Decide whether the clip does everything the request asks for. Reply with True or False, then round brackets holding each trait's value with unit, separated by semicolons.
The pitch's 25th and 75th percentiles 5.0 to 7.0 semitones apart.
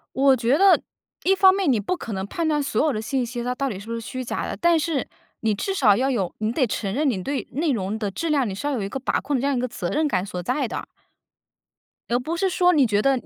True (5.6 semitones)